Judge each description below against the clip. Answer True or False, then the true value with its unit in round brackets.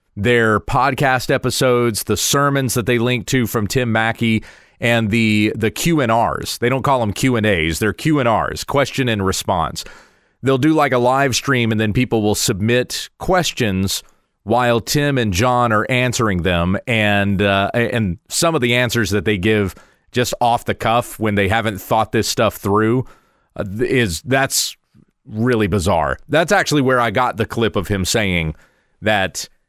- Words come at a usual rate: True (165 wpm)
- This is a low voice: True (115 Hz)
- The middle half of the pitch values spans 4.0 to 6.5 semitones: False (3.3 semitones)